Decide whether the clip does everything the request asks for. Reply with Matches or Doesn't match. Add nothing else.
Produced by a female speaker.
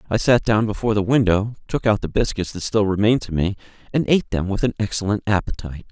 Doesn't match